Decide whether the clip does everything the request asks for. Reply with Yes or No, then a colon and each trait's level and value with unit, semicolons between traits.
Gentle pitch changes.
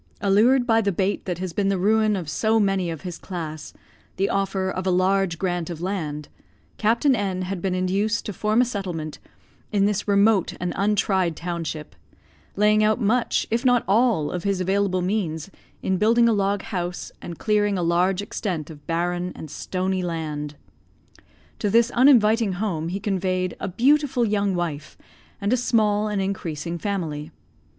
No: average, 3.2 semitones